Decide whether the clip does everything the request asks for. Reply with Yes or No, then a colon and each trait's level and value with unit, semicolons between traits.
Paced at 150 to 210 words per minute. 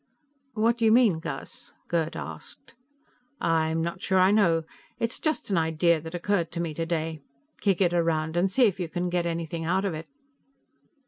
Yes: average, 185 wpm